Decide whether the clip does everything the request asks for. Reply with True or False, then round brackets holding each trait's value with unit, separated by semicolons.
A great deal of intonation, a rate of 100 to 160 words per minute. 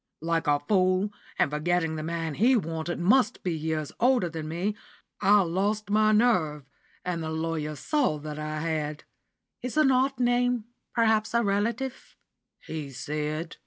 True (5.9 semitones; 155 wpm)